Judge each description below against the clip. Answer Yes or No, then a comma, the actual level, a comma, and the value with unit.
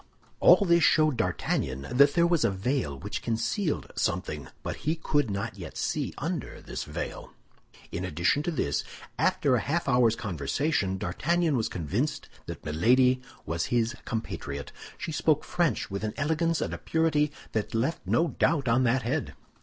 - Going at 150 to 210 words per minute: Yes, average, 165 wpm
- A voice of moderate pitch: No, low, 125 Hz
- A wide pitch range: Yes, wide, 8.0 semitones